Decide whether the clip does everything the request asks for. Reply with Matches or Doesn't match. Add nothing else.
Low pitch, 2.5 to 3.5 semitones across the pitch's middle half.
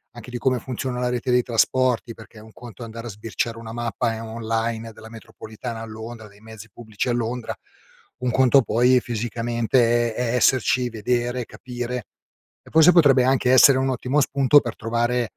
Doesn't match